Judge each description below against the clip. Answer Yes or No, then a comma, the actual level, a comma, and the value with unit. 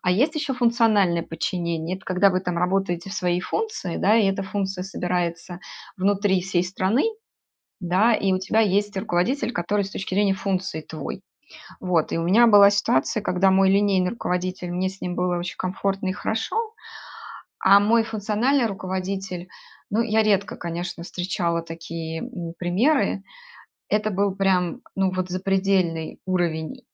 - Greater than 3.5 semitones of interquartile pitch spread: No, narrow, 2.4 semitones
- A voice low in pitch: No, high, 190 Hz